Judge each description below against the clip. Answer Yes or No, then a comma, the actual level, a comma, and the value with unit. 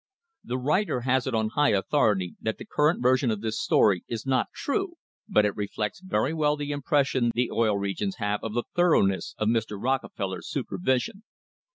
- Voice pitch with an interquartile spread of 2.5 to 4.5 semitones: No, wide, 5.4 semitones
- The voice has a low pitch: Yes, low, 120 Hz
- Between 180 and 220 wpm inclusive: Yes, average, 190 wpm